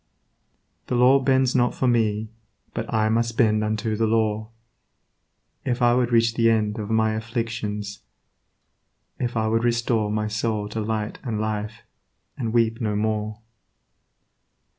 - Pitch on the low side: Yes, low, 110 Hz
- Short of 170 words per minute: Yes, average, 145 wpm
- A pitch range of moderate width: No, narrow, 1.5 semitones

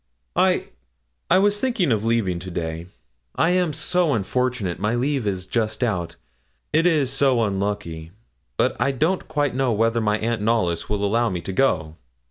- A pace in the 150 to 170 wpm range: Yes, average, 165 wpm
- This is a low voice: Yes, low, 115 Hz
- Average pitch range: No, wide, 6.0 semitones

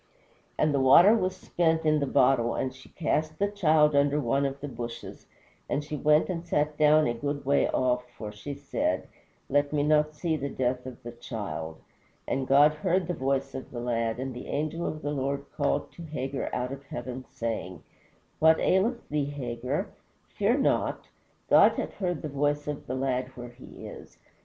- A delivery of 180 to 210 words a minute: Yes, average, 190 wpm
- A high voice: No, medium, 140 Hz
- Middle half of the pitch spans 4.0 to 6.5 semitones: No, average, 3.2 semitones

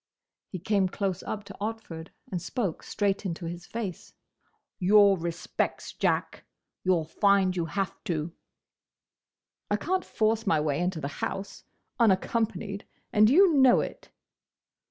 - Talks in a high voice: Yes, high, 195 Hz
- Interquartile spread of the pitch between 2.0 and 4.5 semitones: Yes, average, 3.7 semitones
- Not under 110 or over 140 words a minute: Yes, slow, 135 wpm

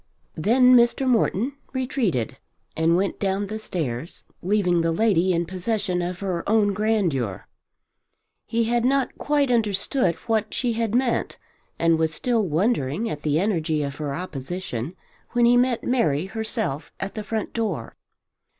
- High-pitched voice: Yes, high, 200 Hz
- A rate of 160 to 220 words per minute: No, average, 145 wpm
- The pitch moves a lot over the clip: Yes, wide, 5.7 semitones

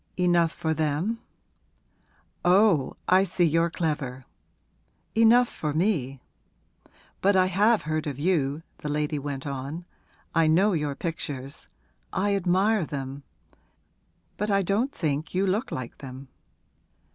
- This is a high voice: No, medium, 165 Hz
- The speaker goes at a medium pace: No, slow, 125 wpm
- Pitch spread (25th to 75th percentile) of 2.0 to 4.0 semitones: No, average, 5.1 semitones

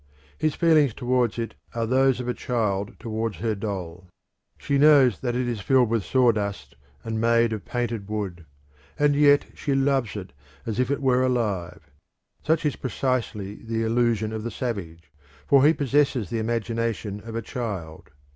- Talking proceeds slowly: No, average, 165 wpm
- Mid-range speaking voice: No, low, 115 Hz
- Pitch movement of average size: Yes, average, 3.6 semitones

